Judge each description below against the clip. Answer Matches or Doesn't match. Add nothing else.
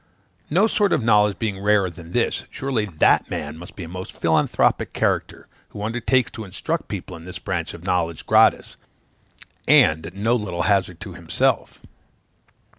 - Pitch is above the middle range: Doesn't match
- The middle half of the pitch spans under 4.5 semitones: Matches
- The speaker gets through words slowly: Doesn't match